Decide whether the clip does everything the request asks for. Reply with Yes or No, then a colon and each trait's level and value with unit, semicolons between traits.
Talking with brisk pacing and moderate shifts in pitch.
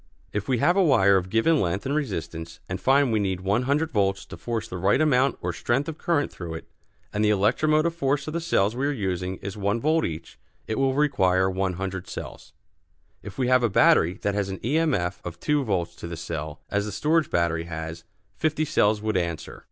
No: fast, 220 wpm; wide, 7.3 semitones